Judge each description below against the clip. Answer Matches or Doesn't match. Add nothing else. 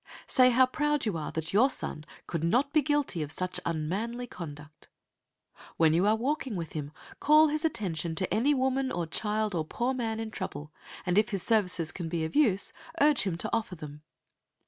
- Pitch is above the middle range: Matches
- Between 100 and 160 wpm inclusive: Doesn't match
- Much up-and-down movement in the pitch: Matches